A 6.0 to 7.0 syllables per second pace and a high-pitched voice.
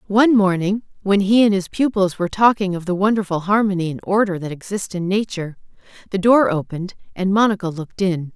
Yes: 6.1 syllables/s; high, 195 Hz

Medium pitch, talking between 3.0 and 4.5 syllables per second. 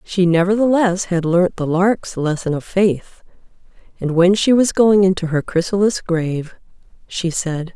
Yes: medium, 180 Hz; 4.4 syllables/s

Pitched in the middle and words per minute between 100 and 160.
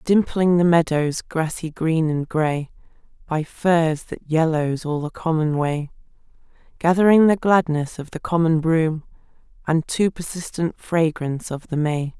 Yes: medium, 160 Hz; average, 145 wpm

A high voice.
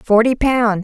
Yes: high, 230 Hz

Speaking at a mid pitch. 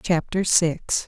Yes: medium, 170 Hz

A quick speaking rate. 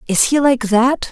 Yes: fast, 215 wpm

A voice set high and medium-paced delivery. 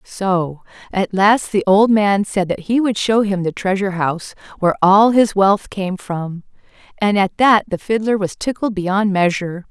Yes: high, 200 Hz; average, 185 wpm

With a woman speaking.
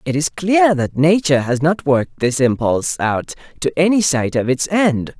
No: male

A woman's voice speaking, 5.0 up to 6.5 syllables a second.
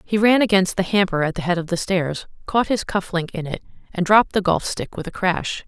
Yes: female; 5.5 syllables/s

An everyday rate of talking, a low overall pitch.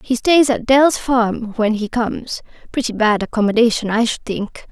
No: average, 165 wpm; high, 230 Hz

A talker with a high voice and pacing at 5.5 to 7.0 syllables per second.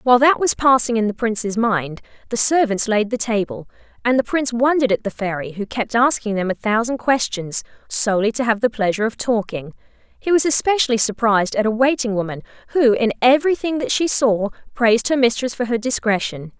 Yes: high, 230 Hz; 5.9 syllables/s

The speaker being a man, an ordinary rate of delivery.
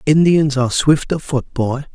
Yes: male; average, 185 wpm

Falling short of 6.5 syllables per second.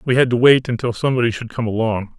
No: 6.8 syllables/s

